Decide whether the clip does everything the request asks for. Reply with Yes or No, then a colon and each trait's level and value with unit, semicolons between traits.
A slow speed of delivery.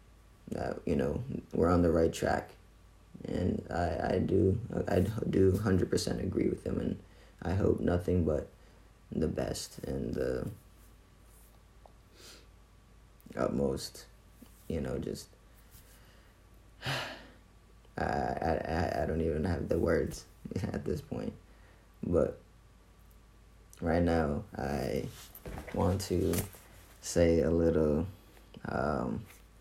Yes: slow, 105 wpm